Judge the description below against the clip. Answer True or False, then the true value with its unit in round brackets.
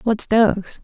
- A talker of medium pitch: False (215 Hz)